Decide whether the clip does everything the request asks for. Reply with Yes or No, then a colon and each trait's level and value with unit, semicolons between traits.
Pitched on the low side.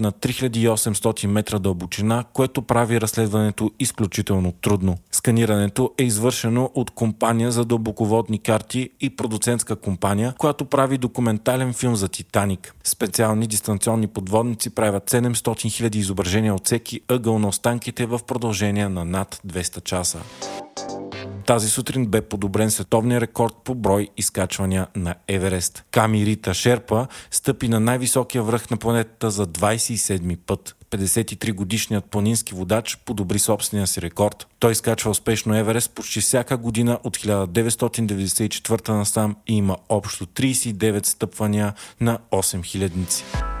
Yes: low, 110 Hz